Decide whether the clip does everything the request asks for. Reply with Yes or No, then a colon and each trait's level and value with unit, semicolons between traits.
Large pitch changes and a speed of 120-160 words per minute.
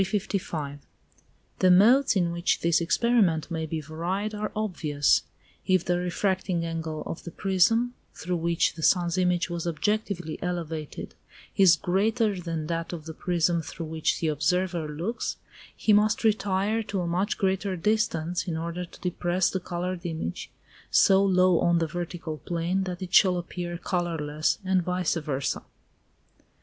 No: narrow, 2.5 semitones; average, 150 wpm